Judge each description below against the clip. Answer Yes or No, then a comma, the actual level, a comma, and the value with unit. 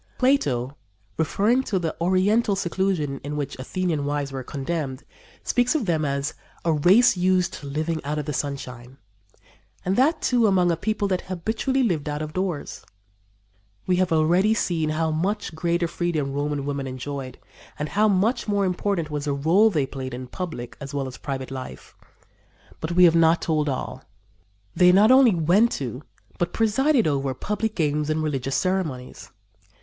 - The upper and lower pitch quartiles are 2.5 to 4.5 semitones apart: No, average, 5.1 semitones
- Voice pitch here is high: No, medium, 165 Hz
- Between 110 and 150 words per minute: No, average, 170 wpm